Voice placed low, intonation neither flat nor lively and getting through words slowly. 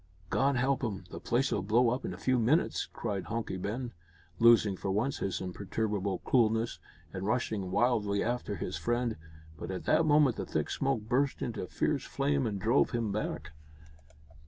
No: low, 115 Hz; average, 4.0 semitones; average, 170 wpm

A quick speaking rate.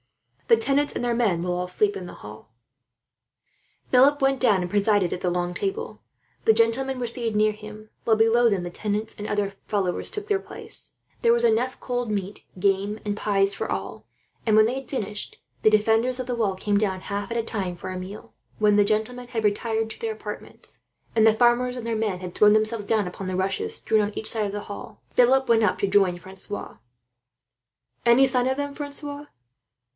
Yes: fast, 210 wpm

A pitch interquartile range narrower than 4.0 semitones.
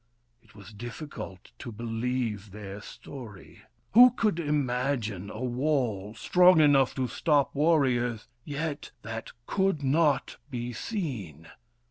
No: average, 5.3 semitones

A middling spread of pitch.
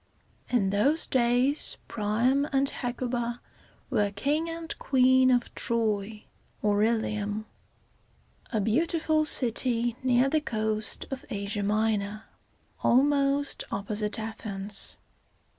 Yes: average, 4.2 semitones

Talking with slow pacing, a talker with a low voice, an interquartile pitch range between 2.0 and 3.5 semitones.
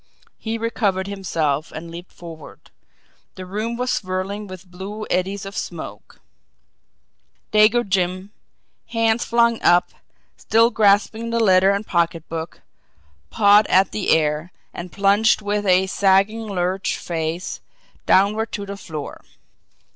No: slow, 120 wpm; high, 195 Hz; average, 3.1 semitones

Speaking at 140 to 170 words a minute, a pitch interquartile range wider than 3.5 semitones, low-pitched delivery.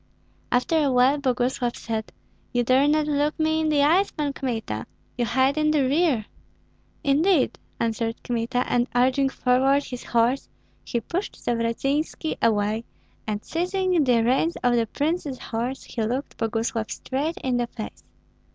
No: average, 150 wpm; average, 4.0 semitones; very high, 255 Hz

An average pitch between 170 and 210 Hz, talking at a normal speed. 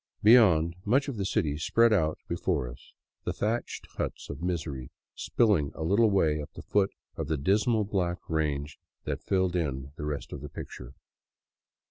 No: very low, 85 Hz; average, 175 wpm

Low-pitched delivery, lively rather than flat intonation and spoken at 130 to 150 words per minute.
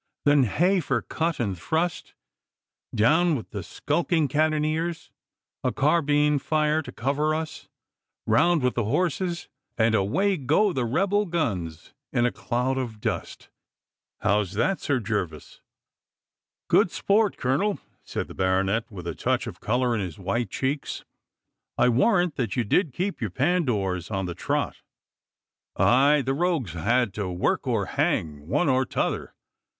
Yes: low, 130 Hz; wide, 7.0 semitones; average, 145 wpm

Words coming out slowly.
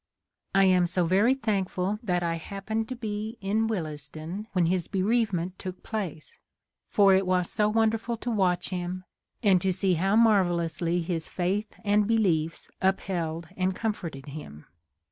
No: average, 160 wpm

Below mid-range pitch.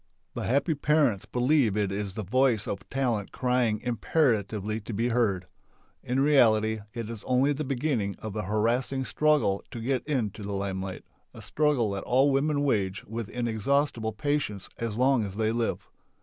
Yes: low, 115 Hz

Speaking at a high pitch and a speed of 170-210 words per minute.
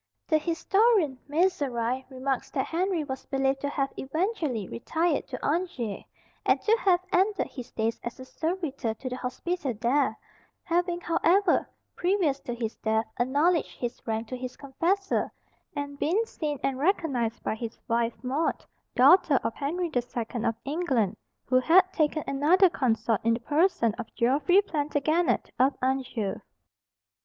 No: very high, 280 Hz; average, 150 wpm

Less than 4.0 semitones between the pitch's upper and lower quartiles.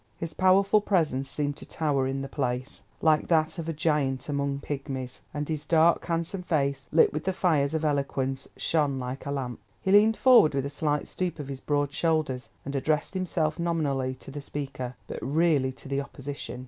Yes: average, 3.0 semitones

